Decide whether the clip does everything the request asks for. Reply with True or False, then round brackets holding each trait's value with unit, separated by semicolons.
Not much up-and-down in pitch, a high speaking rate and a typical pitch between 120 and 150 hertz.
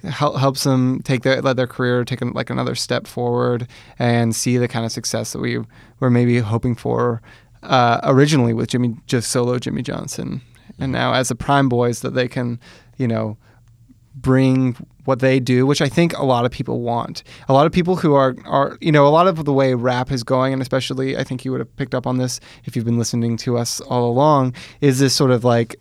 True (1.9 semitones; 225 wpm; 125 Hz)